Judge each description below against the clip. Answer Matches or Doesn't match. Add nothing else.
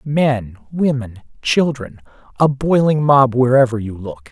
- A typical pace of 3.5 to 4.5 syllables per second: Matches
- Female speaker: Doesn't match